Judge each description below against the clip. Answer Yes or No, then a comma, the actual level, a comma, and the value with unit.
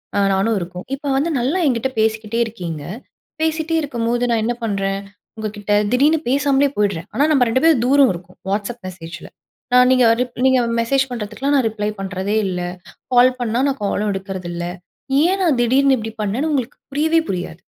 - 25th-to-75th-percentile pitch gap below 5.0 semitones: No, average, 5.3 semitones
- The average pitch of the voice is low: No, high, 230 Hz